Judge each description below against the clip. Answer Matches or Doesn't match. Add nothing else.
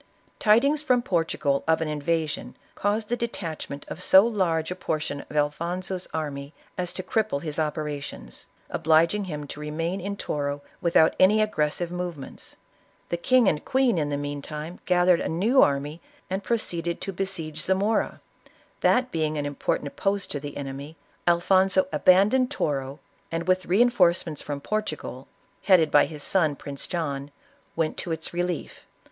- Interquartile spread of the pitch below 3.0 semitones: Doesn't match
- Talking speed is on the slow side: Doesn't match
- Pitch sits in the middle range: Matches